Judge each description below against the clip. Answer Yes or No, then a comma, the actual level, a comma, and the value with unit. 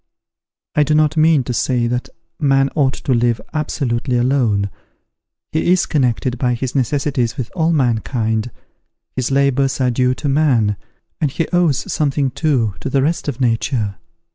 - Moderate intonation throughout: Yes, average, 3.5 semitones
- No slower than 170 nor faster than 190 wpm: No, average, 160 wpm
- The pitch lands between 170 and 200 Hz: No, low, 130 Hz